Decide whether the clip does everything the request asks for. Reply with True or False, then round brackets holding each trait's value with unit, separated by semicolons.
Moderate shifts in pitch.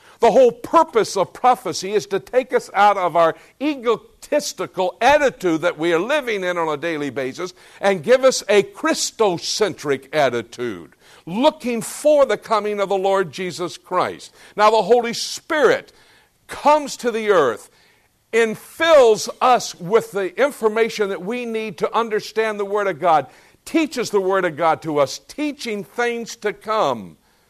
False (5.7 semitones)